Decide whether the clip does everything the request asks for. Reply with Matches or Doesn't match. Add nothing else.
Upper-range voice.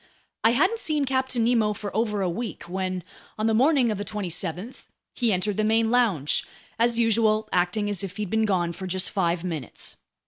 Matches